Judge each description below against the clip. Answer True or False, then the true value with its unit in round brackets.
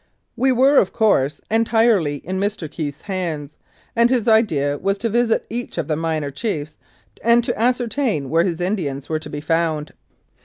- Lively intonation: True (7.1 semitones)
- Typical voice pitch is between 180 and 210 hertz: True (185 Hz)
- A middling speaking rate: True (180 wpm)